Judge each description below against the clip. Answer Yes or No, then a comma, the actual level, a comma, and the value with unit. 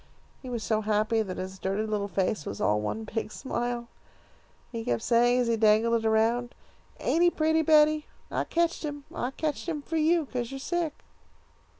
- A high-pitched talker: Yes, high, 235 Hz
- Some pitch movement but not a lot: No, wide, 5.8 semitones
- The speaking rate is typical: Yes, average, 190 wpm